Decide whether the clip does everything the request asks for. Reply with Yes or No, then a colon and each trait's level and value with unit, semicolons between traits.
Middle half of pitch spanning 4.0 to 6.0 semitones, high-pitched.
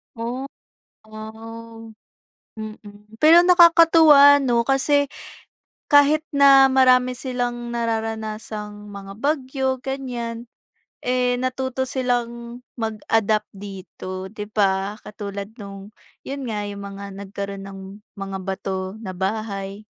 Yes: average, 4.4 semitones; high, 225 Hz